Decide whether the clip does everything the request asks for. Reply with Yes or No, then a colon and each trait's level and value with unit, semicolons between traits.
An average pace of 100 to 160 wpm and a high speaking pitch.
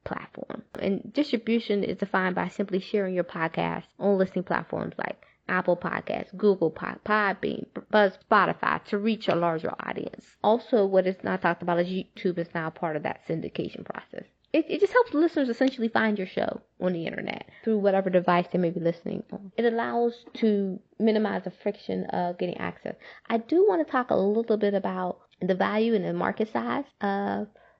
No: average, 185 wpm; high, 200 Hz